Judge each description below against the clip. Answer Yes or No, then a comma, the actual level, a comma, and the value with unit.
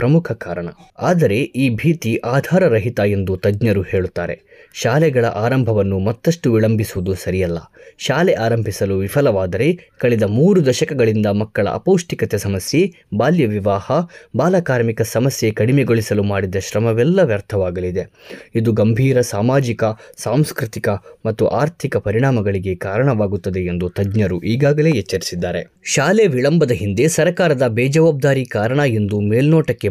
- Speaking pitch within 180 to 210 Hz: No, low, 115 Hz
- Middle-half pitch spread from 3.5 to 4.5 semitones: No, wide, 5.6 semitones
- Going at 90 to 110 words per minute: Yes, average, 100 wpm